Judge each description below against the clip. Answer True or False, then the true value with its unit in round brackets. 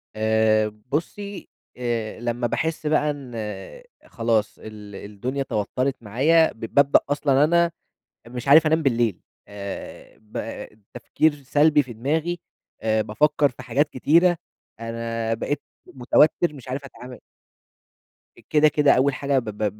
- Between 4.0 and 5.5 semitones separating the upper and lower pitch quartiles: True (4.8 semitones)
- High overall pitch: False (130 Hz)